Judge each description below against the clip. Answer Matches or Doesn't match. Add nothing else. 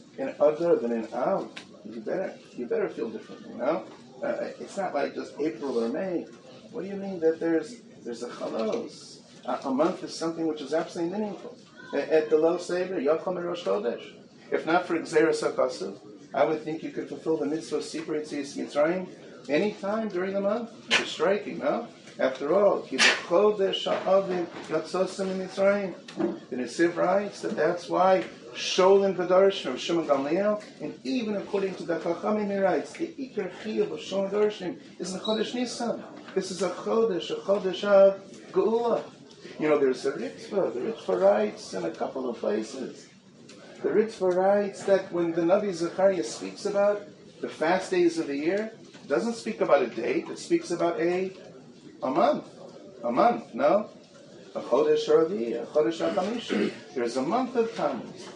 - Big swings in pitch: Doesn't match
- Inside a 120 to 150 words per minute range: Doesn't match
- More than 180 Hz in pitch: Matches